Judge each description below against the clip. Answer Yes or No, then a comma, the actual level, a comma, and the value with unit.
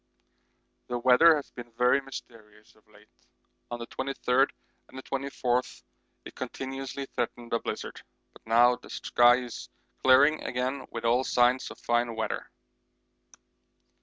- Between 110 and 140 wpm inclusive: Yes, slow, 135 wpm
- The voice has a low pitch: Yes, low, 125 Hz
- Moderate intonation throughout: No, narrow, 2.0 semitones